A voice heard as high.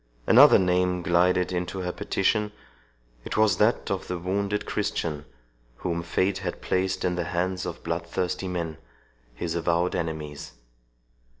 No: very low, 90 Hz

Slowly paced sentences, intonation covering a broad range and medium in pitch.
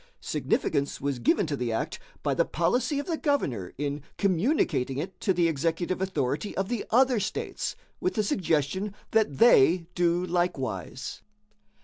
No: average, 150 wpm; wide, 6.6 semitones; medium, 175 Hz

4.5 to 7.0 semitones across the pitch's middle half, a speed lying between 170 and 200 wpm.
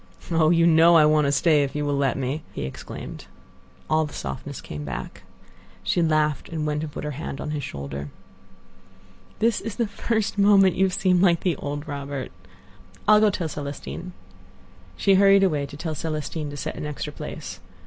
No: average, 4.0 semitones; average, 190 wpm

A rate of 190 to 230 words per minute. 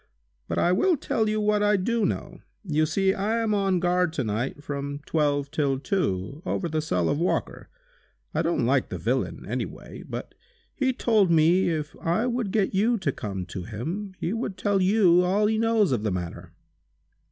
Yes: average, 195 wpm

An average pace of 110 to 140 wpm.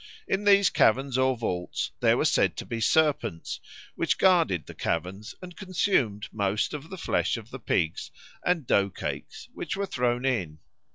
No: average, 170 wpm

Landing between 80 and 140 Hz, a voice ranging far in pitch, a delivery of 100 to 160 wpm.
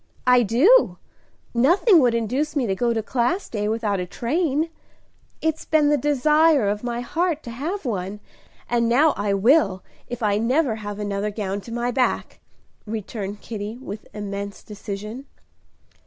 No: high, 235 Hz; wide, 5.7 semitones; average, 155 wpm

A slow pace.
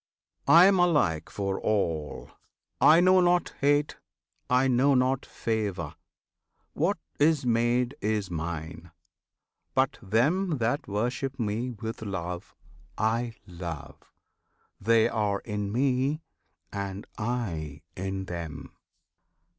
Yes: slow, 105 wpm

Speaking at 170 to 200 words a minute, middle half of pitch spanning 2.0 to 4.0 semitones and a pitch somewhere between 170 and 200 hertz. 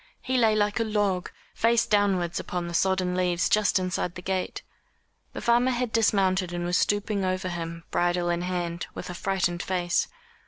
Yes: average, 180 wpm; average, 2.8 semitones; medium, 185 Hz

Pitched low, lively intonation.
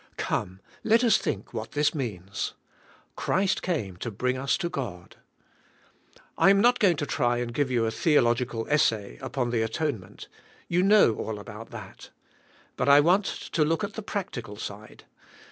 Yes: low, 125 Hz; wide, 7.3 semitones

